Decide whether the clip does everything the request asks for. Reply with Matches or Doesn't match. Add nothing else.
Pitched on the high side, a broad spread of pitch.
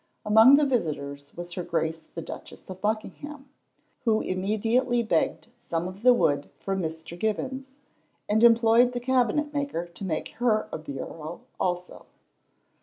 Matches